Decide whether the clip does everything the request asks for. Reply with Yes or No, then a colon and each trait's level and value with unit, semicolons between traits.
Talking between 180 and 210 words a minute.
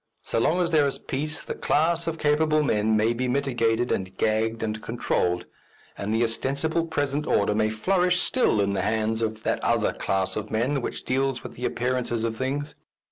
Yes: average, 190 wpm